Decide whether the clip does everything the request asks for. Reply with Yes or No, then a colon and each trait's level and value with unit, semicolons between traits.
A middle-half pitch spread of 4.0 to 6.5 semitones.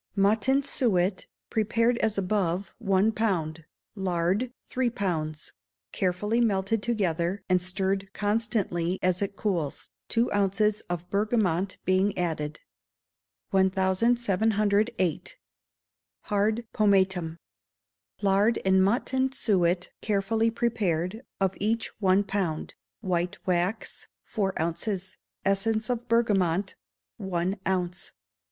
No: average, 3.2 semitones